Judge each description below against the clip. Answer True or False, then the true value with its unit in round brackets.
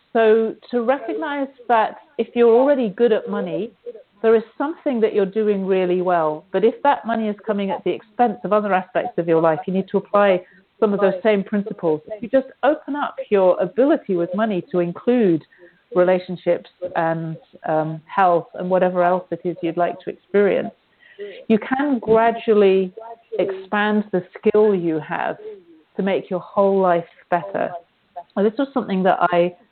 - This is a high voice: True (205 Hz)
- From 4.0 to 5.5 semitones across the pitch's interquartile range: True (4.3 semitones)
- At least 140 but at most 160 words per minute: False (175 wpm)